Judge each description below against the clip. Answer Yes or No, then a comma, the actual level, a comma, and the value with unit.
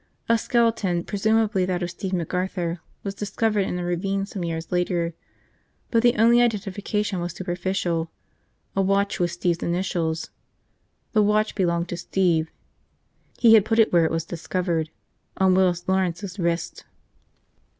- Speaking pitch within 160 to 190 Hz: Yes, medium, 185 Hz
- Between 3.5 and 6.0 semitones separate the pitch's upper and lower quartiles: No, average, 2.9 semitones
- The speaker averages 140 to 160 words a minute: Yes, average, 150 wpm